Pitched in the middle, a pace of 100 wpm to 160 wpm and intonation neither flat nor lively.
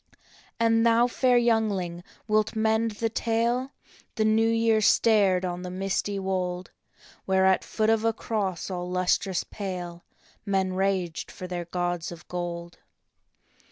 No: high, 195 Hz; average, 150 wpm; average, 3.8 semitones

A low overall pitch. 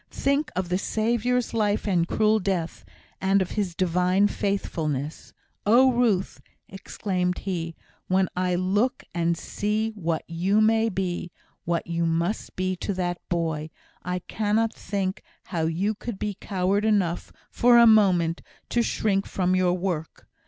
No: high, 190 Hz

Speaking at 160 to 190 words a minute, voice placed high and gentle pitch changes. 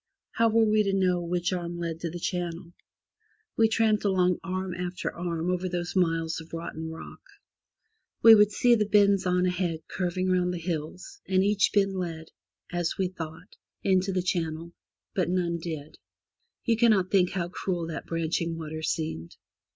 No: average, 170 wpm; medium, 180 Hz; narrow, 2.3 semitones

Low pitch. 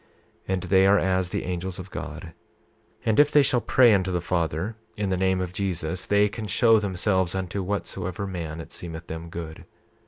Yes: very low, 95 Hz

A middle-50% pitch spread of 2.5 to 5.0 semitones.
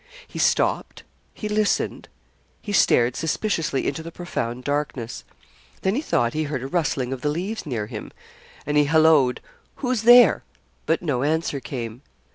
No: wide, 5.5 semitones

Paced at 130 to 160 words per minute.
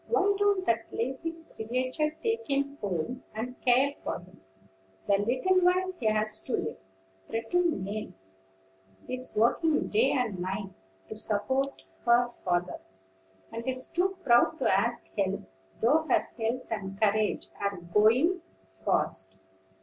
Yes: slow, 135 wpm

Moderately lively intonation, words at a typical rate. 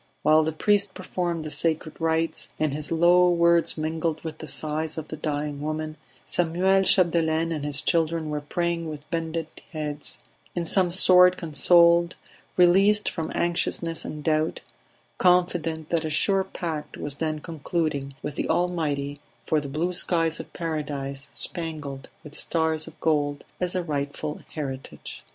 No: narrow, 2.2 semitones; average, 150 wpm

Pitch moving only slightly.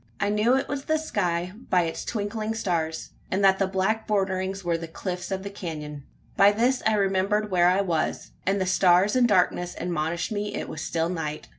No: average, 3.1 semitones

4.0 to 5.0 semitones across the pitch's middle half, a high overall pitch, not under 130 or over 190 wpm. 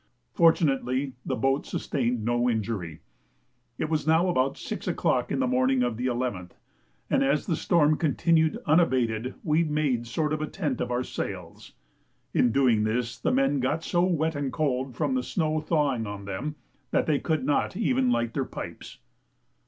No: average, 4.3 semitones; low, 135 Hz; average, 175 wpm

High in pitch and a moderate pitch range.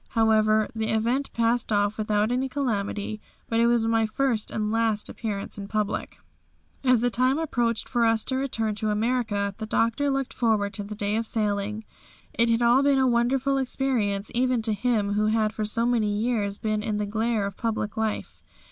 No: high, 225 Hz; narrow, 2.3 semitones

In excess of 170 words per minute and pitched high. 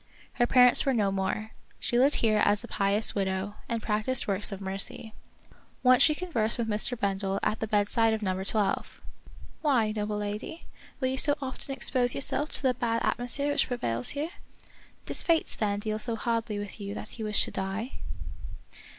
Yes: average, 195 wpm; high, 220 Hz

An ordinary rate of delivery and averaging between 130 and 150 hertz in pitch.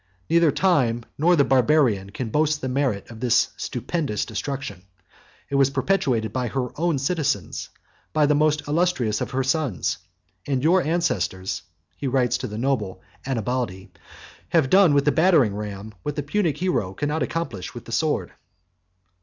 Yes: average, 160 wpm; low, 135 Hz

